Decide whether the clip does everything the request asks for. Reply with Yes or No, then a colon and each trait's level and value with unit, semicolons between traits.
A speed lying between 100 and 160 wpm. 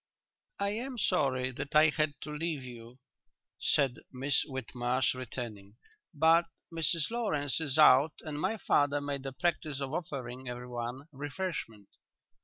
Yes: slow, 135 wpm